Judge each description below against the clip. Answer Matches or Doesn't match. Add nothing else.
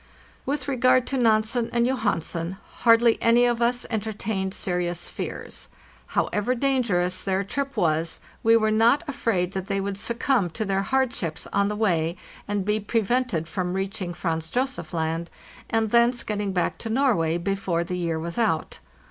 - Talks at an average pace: Matches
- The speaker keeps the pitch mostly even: Doesn't match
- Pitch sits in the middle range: Doesn't match